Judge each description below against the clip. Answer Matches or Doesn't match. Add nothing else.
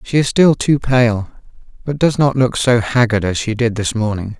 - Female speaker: Doesn't match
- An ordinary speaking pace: Doesn't match